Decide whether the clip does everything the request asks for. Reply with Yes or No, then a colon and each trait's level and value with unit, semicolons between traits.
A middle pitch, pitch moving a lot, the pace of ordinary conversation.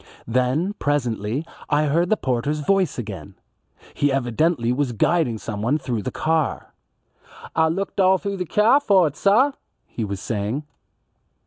Yes: medium, 145 Hz; wide, 6.9 semitones; average, 145 wpm